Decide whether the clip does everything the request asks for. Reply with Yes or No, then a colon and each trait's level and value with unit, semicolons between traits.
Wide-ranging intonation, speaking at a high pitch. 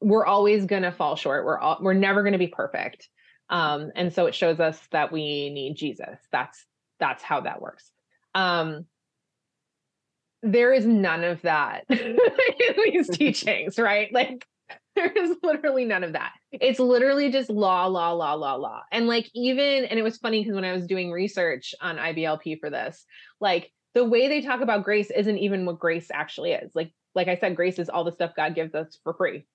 Yes: wide, 6.4 semitones; high, 200 Hz